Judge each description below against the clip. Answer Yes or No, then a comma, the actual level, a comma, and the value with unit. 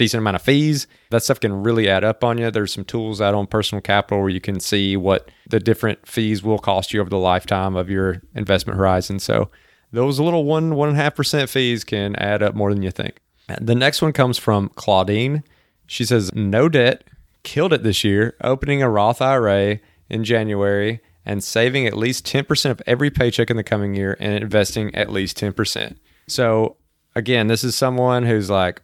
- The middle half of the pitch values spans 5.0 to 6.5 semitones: No, average, 3.5 semitones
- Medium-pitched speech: No, low, 110 Hz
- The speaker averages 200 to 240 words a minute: Yes, fast, 205 wpm